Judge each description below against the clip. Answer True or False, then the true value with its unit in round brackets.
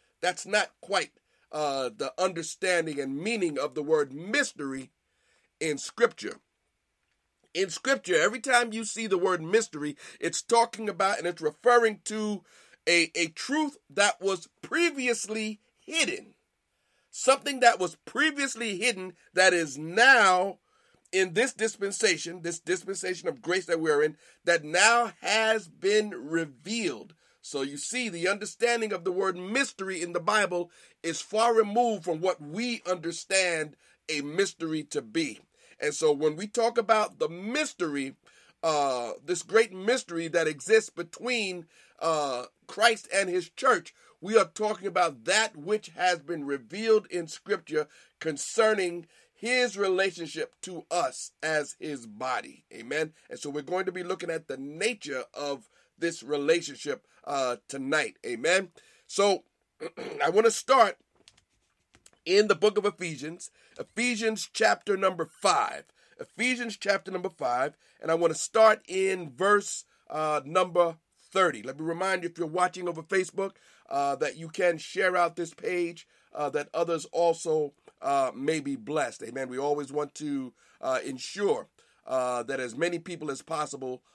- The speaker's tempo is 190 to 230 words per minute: False (145 wpm)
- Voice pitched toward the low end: False (185 Hz)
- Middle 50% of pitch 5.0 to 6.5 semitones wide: True (5.3 semitones)